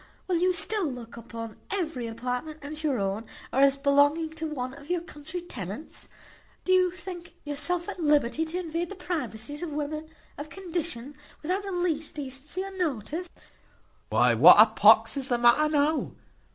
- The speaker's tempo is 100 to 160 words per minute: No, average, 170 wpm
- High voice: Yes, very high, 305 Hz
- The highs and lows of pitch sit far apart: No, average, 4.6 semitones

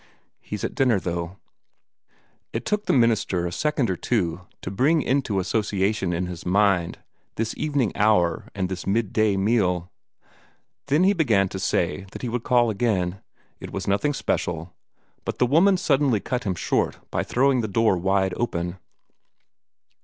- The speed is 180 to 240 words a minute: No, average, 160 wpm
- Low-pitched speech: Yes, low, 100 Hz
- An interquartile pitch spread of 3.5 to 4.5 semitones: No, average, 5.2 semitones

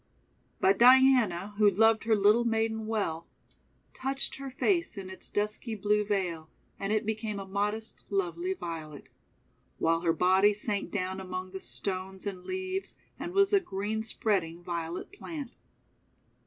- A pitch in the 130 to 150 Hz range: No, high, 205 Hz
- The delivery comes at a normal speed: Yes, average, 145 wpm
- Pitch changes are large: No, average, 3.3 semitones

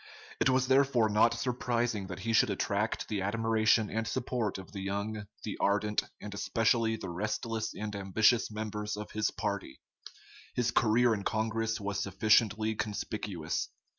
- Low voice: Yes, low, 110 Hz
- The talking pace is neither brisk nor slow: Yes, average, 150 wpm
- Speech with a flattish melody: Yes, narrow, 1.8 semitones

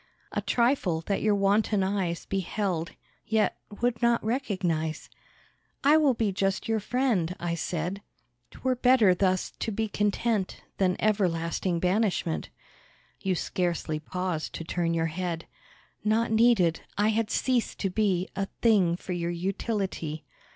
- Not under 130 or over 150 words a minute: Yes, slow, 135 wpm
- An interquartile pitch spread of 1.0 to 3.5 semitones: No, average, 4.1 semitones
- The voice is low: No, high, 195 Hz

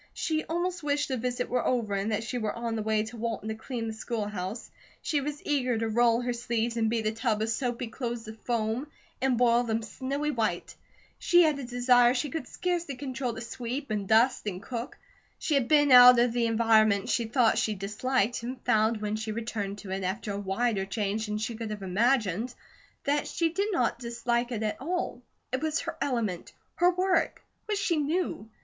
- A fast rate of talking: Yes, fast, 210 wpm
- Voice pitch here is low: No, high, 235 Hz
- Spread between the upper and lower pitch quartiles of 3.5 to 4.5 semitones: No, average, 3.1 semitones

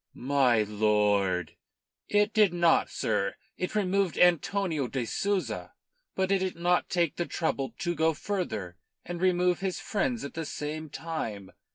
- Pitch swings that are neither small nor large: No, wide, 7.9 semitones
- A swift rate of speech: No, average, 150 wpm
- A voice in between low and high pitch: Yes, medium, 165 Hz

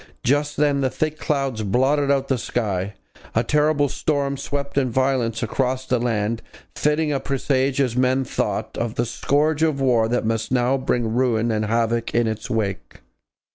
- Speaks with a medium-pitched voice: No, low, 130 Hz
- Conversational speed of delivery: Yes, average, 170 wpm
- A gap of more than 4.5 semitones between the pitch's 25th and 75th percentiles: No, average, 3.5 semitones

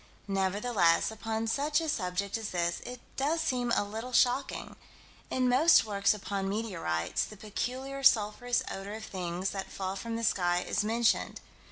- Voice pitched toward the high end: Yes, high, 215 Hz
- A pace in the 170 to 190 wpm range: No, average, 160 wpm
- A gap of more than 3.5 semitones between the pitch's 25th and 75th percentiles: Yes, average, 4.2 semitones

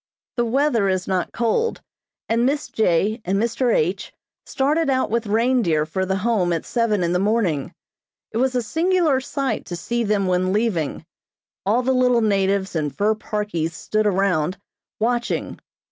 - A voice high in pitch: Yes, high, 215 Hz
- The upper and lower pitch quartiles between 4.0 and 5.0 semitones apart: Yes, average, 4.4 semitones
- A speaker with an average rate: Yes, average, 160 wpm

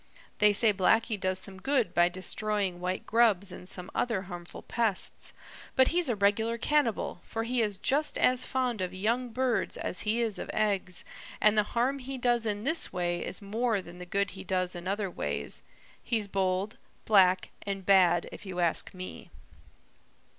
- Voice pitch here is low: No, high, 205 Hz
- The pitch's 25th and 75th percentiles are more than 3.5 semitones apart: Yes, average, 4.0 semitones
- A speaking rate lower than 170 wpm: No, average, 180 wpm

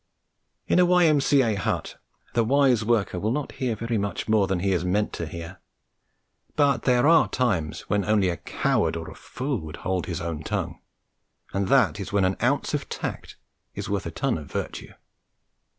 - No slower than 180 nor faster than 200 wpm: Yes, average, 185 wpm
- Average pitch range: No, wide, 5.8 semitones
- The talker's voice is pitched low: Yes, low, 105 Hz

